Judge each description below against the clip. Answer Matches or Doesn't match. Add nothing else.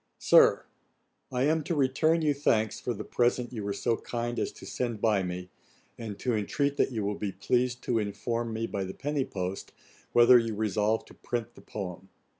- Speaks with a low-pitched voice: Matches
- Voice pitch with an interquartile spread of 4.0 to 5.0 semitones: Doesn't match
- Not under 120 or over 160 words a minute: Doesn't match